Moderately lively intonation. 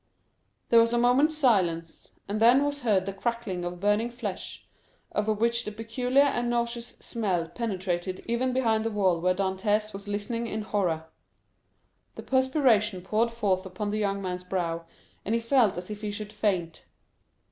Yes: average, 3.9 semitones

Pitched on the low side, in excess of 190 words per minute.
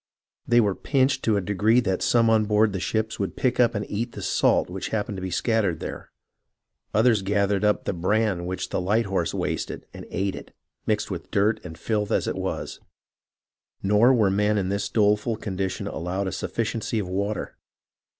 Yes: low, 105 Hz; average, 200 wpm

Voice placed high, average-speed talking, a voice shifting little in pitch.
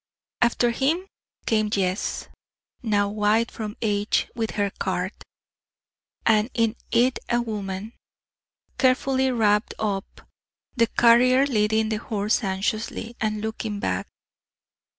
No: high, 220 Hz; slow, 110 wpm; narrow, 2.3 semitones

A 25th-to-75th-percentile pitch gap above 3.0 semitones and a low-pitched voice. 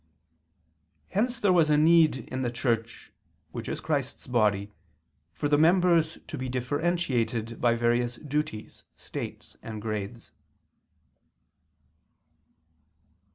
Yes: wide, 5.5 semitones; low, 130 Hz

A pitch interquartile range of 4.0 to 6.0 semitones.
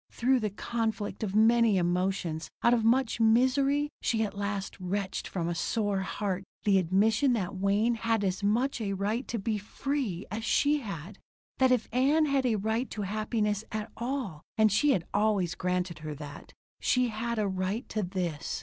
No: average, 3.6 semitones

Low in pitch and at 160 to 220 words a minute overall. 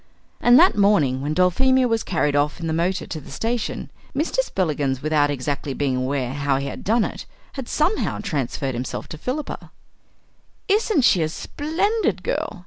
No: medium, 170 Hz; average, 170 wpm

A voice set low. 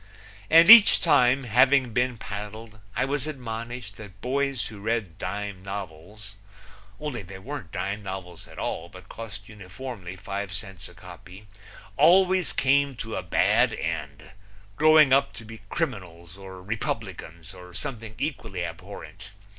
Yes: low, 105 Hz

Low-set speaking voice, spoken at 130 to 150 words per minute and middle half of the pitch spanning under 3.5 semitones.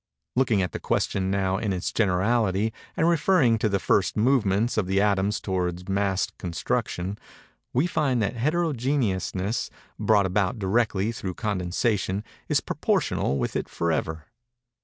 No: low, 100 Hz; average, 140 wpm; average, 3.8 semitones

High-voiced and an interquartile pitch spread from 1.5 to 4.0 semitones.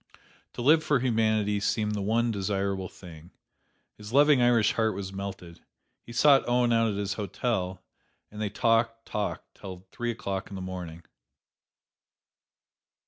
No: low, 105 Hz; average, 3.3 semitones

